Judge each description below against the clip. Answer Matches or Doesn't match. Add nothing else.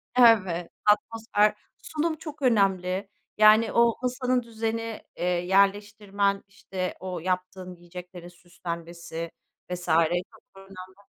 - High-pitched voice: Matches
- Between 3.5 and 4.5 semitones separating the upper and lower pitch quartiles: Matches